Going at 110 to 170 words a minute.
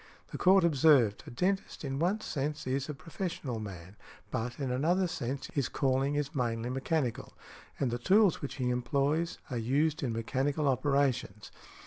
Yes: average, 165 wpm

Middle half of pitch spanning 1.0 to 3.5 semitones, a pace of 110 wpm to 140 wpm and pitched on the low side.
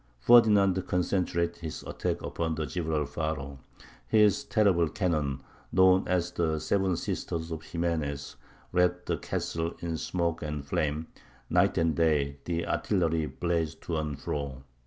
Yes: average, 2.7 semitones; slow, 135 wpm; very low, 85 Hz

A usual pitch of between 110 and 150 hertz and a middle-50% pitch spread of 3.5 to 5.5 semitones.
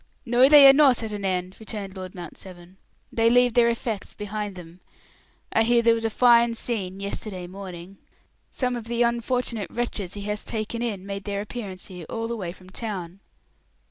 No: high, 210 Hz; average, 3.8 semitones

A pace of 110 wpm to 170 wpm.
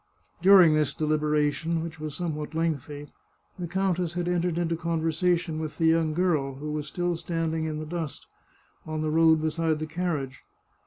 Yes: average, 165 wpm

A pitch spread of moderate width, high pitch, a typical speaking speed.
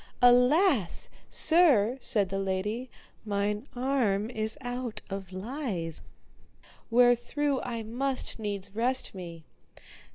No: average, 4.2 semitones; high, 230 Hz; slow, 100 wpm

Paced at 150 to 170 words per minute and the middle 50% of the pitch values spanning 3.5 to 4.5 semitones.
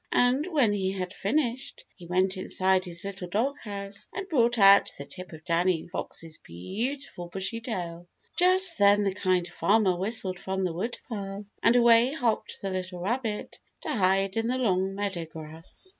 Yes: average, 165 wpm; average, 4.2 semitones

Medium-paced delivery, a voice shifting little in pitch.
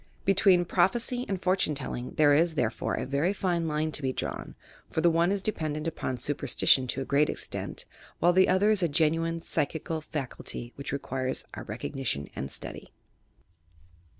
No: average, 170 wpm; average, 4.2 semitones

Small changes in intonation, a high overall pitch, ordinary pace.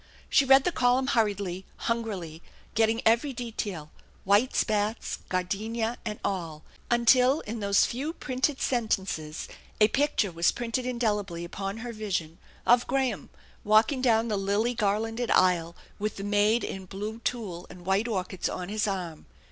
No: average, 3.7 semitones; high, 215 Hz; average, 150 wpm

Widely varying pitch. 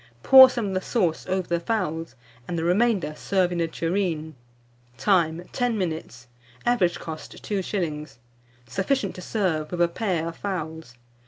No: average, 3.7 semitones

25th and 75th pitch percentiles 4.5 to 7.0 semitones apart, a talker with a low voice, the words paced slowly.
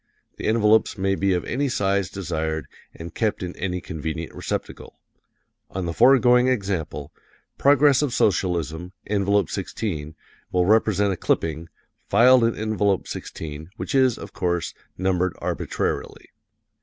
Yes: average, 4.8 semitones; very low, 95 Hz; slow, 130 wpm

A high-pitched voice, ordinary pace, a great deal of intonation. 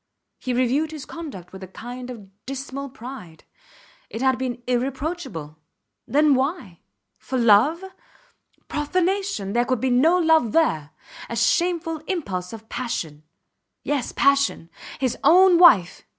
No: very high, 260 Hz; slow, 130 wpm; wide, 6.0 semitones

